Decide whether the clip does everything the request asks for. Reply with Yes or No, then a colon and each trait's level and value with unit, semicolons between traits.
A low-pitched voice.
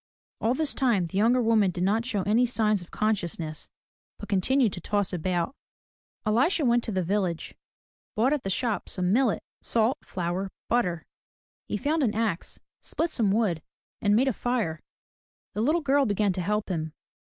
No: high, 210 Hz